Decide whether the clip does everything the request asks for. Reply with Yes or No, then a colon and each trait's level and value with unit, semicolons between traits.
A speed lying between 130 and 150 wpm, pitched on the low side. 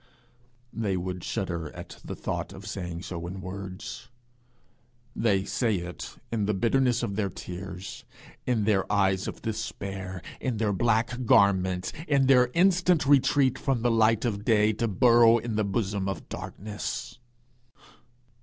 Yes: average, 145 wpm; low, 105 Hz